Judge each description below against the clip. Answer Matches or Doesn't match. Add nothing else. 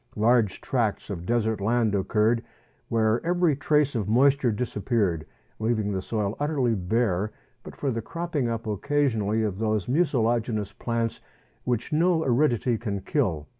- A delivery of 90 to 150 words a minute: Matches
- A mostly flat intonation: Doesn't match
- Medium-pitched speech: Doesn't match